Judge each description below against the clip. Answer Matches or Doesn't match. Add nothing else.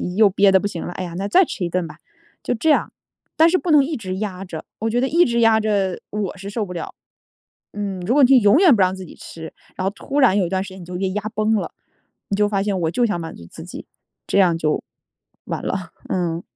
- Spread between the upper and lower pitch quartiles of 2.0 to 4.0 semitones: Matches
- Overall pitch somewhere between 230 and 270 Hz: Doesn't match